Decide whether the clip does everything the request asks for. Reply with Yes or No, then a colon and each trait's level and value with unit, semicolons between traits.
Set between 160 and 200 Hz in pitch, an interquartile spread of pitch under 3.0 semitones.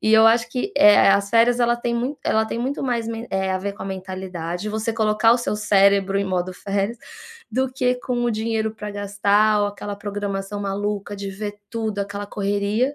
No: high, 210 Hz; narrow, 2.4 semitones